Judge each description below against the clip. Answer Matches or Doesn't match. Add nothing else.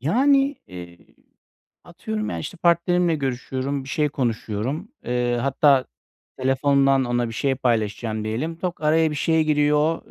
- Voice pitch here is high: Doesn't match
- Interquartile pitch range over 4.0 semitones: Matches